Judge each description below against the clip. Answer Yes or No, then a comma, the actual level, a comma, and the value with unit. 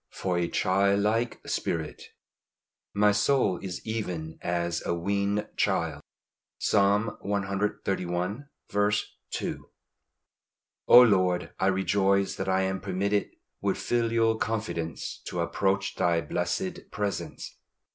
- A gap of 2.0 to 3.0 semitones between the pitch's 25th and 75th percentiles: Yes, narrow, 2.5 semitones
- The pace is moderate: No, slow, 105 wpm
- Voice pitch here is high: No, low, 100 Hz